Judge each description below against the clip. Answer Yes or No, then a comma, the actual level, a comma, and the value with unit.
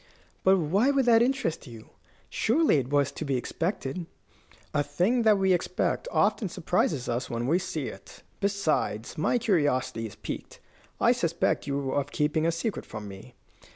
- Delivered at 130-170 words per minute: Yes, average, 165 wpm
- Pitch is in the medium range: Yes, medium, 160 Hz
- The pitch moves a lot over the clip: Yes, wide, 6.7 semitones